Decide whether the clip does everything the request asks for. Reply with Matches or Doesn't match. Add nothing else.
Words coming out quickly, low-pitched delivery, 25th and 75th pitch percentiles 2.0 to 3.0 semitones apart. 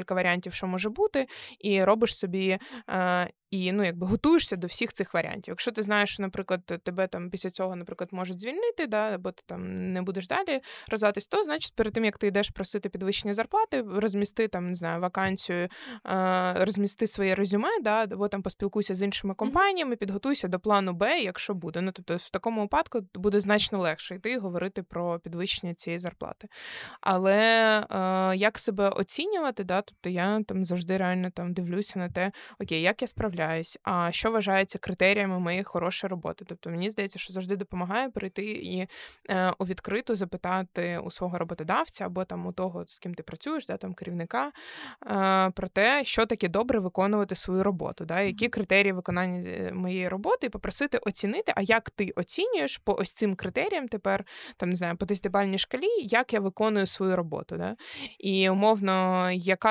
Doesn't match